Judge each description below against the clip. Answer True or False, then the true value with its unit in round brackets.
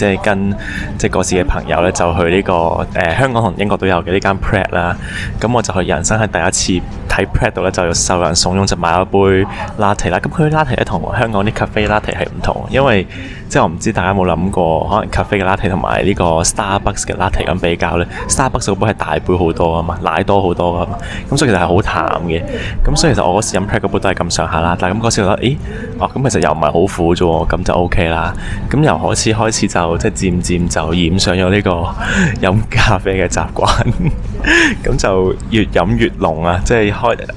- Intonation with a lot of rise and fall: False (2.9 semitones)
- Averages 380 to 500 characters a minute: True (395 characters per minute)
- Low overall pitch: True (95 Hz)